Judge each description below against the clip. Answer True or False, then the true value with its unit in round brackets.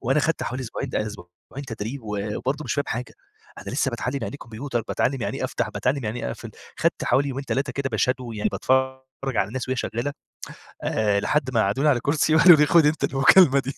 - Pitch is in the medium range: False (130 Hz)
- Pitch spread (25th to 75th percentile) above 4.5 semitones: False (3.8 semitones)